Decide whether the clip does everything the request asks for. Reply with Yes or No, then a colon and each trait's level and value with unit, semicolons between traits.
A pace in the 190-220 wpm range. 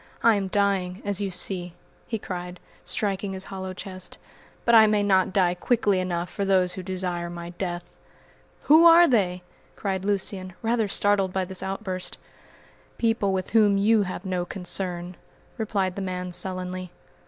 No: average, 160 wpm